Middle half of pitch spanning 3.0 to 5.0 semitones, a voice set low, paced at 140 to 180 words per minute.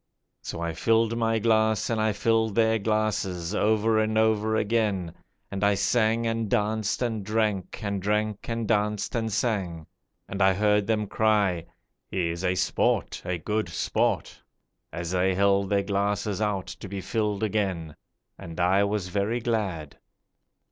No: narrow, 2.4 semitones; low, 105 Hz; average, 155 wpm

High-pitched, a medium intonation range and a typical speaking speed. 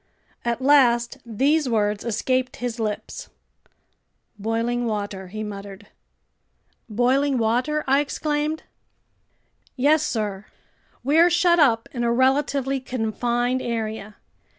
No: high, 240 Hz; average, 4.0 semitones; slow, 105 wpm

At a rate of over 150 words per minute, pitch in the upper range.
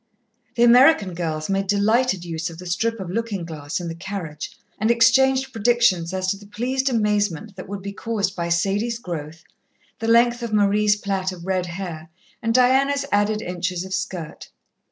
Yes: average, 175 wpm; high, 200 Hz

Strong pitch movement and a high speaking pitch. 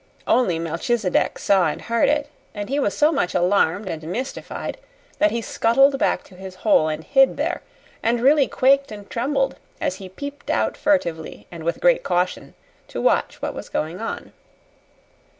Yes: wide, 7.4 semitones; high, 220 Hz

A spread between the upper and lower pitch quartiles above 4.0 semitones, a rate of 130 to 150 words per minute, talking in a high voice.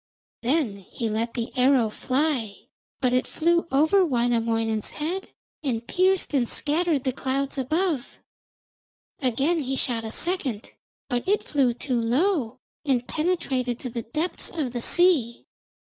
Yes: average, 4.9 semitones; average, 140 wpm; very high, 260 Hz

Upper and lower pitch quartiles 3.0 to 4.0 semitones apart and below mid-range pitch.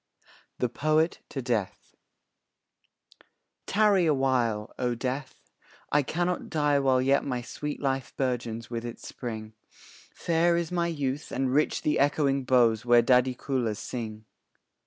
Yes: average, 3.6 semitones; low, 130 Hz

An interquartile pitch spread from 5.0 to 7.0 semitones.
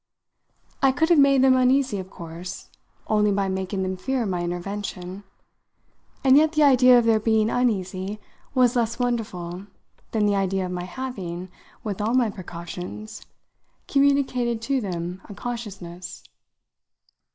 Yes: average, 5.3 semitones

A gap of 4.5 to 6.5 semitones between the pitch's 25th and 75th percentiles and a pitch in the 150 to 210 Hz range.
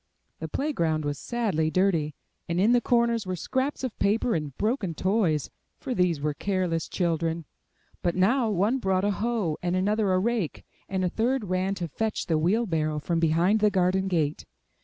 Yes: average, 4.9 semitones; medium, 185 Hz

